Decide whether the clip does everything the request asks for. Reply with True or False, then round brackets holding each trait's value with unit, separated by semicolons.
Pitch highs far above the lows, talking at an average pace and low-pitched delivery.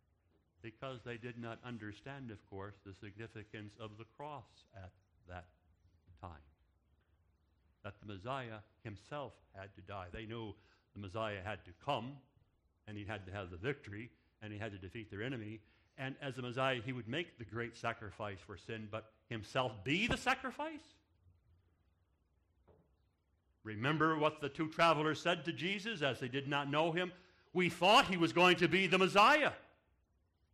True (7.1 semitones; 165 wpm; 110 Hz)